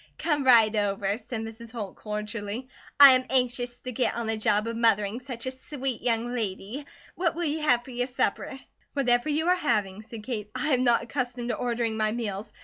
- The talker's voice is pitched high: Yes, high, 240 Hz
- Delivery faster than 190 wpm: Yes, fast, 205 wpm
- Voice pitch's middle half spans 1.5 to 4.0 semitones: Yes, average, 3.1 semitones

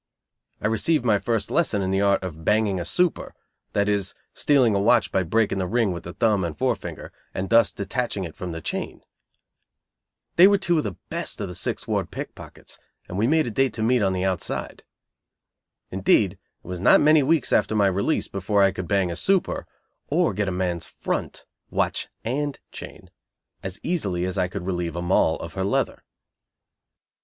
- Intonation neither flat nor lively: Yes, average, 4.6 semitones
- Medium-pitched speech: No, low, 100 Hz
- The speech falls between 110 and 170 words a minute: No, average, 195 wpm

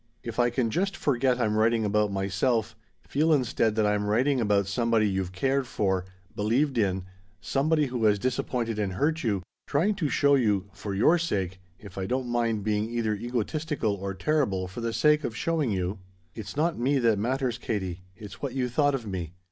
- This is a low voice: Yes, low, 115 Hz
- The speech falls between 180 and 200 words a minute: Yes, average, 190 wpm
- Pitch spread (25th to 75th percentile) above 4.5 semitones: Yes, average, 4.9 semitones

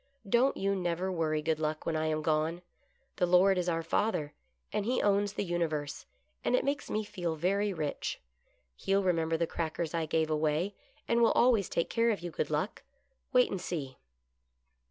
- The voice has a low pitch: No, medium, 175 Hz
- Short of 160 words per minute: No, average, 185 wpm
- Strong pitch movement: No, average, 4.1 semitones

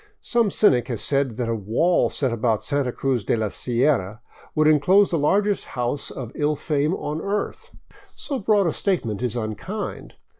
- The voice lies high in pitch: No, medium, 140 Hz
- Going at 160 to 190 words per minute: Yes, average, 175 wpm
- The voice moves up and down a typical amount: No, wide, 7.3 semitones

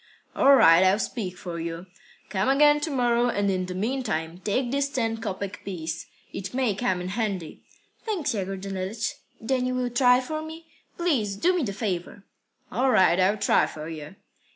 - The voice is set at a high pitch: Yes, high, 210 Hz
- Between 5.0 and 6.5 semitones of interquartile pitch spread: Yes, wide, 5.5 semitones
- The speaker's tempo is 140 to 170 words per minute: No, average, 180 wpm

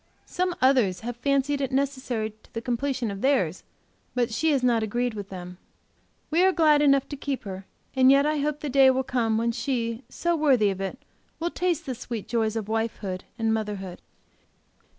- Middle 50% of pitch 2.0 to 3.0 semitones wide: No, average, 4.2 semitones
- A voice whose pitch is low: No, high, 245 Hz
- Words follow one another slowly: No, average, 195 wpm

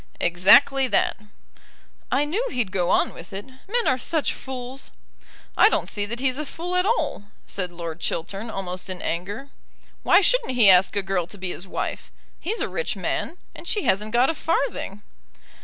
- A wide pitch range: Yes, wide, 7.5 semitones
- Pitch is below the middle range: No, high, 235 Hz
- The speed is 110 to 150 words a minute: No, average, 185 wpm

